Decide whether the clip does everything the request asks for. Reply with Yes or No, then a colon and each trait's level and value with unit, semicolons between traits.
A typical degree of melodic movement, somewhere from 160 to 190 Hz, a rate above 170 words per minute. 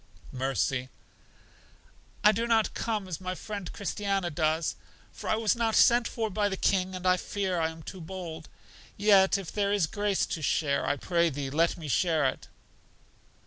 Yes: average, 4.3 semitones; medium, 185 Hz; average, 180 wpm